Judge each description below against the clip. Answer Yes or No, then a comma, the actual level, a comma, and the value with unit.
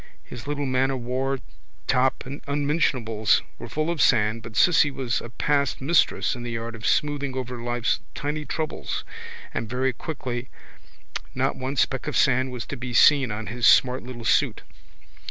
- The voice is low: Yes, low, 130 Hz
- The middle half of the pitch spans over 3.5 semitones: No, average, 2.9 semitones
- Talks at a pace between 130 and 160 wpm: No, average, 170 wpm